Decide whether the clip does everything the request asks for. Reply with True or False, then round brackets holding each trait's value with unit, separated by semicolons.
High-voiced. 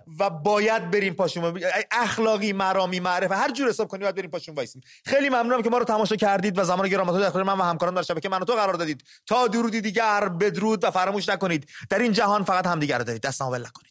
True (195 Hz)